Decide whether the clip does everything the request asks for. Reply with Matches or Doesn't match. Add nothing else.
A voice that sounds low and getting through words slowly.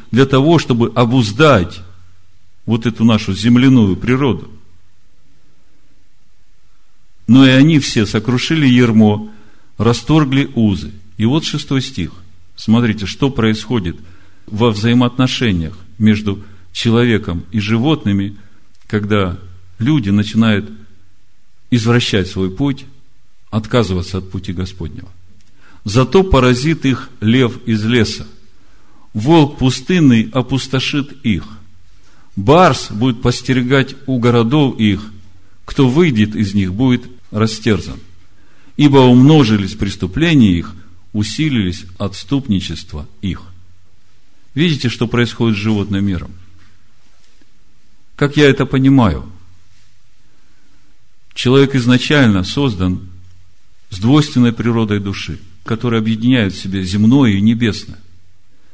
Matches